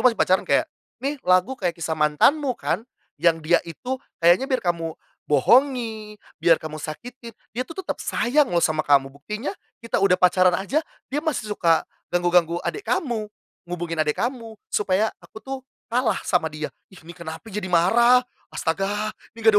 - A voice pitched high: Yes, high, 195 Hz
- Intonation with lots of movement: Yes, wide, 6.2 semitones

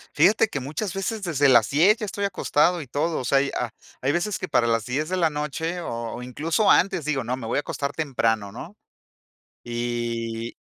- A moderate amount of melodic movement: No, wide, 6.4 semitones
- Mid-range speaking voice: Yes, medium, 145 Hz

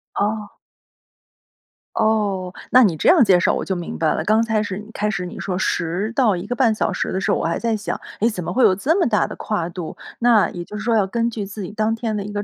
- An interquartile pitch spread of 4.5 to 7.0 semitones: No, average, 3.3 semitones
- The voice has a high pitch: Yes, high, 210 Hz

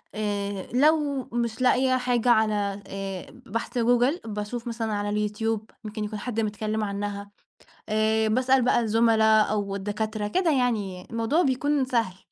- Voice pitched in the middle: No, high, 220 Hz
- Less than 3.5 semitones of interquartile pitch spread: Yes, average, 3.0 semitones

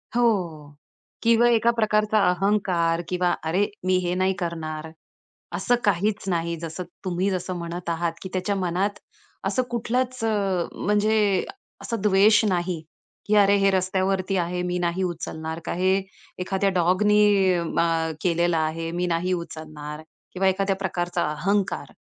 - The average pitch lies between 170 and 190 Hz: Yes, medium, 185 Hz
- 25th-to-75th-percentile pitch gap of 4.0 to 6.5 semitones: No, average, 2.9 semitones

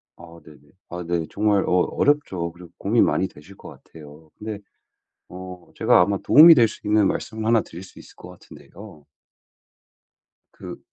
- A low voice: Yes, very low, 95 Hz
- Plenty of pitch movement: No, average, 4.1 semitones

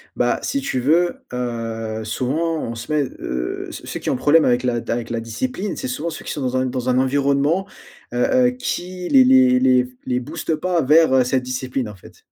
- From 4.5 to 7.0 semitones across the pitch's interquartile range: Yes, average, 4.8 semitones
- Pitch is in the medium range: No, low, 130 Hz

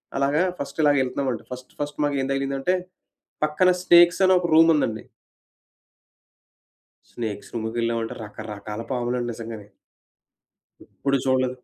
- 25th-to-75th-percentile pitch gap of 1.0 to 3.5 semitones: No, average, 4.0 semitones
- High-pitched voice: No, low, 130 Hz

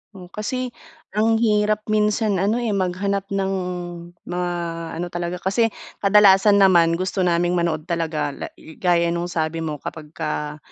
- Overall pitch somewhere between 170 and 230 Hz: Yes, medium, 185 Hz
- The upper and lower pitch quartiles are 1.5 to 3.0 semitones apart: No, average, 3.6 semitones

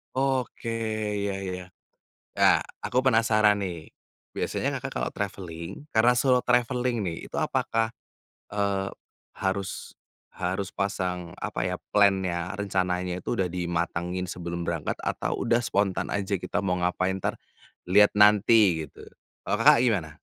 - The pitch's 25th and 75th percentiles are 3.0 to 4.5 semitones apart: Yes, average, 3.4 semitones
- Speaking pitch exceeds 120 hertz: No, very low, 95 Hz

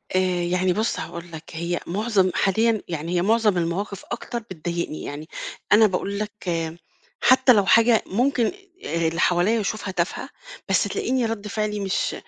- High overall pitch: Yes, high, 200 Hz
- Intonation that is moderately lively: Yes, average, 4.2 semitones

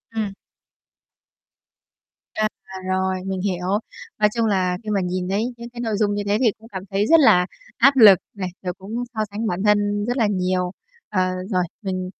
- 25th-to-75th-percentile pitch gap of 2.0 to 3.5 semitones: Yes, average, 2.8 semitones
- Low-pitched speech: No, high, 200 Hz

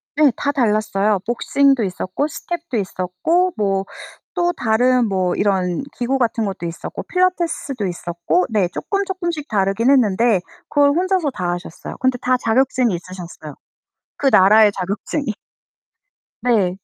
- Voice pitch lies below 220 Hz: No, high, 225 Hz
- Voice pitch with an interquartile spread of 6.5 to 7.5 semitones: Yes, wide, 6.9 semitones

